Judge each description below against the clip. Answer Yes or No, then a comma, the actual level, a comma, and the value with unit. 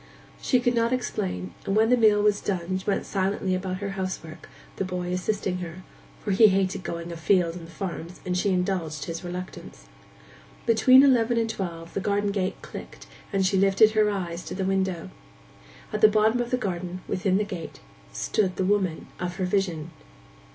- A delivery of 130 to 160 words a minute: No, average, 185 wpm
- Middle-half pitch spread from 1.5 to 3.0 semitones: Yes, average, 2.7 semitones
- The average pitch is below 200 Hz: Yes, high, 190 Hz